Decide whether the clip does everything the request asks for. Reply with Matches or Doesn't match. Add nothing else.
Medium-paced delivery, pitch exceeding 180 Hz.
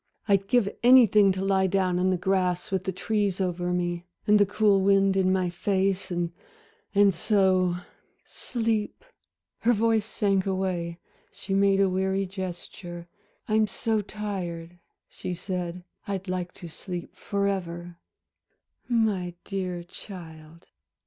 Doesn't match